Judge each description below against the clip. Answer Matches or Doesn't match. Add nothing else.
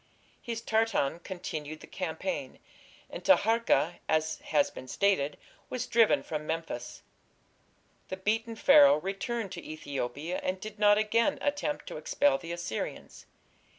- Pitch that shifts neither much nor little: Doesn't match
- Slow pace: Matches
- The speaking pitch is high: Matches